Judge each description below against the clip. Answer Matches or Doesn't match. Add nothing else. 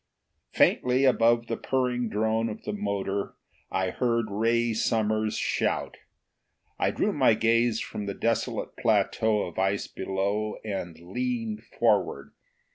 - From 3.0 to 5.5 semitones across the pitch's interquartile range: Doesn't match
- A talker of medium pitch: Doesn't match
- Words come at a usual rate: Doesn't match